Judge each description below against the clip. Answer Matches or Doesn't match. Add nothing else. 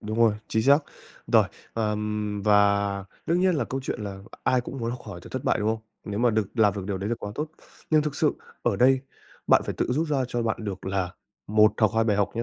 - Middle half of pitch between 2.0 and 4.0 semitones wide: Matches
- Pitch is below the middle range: Matches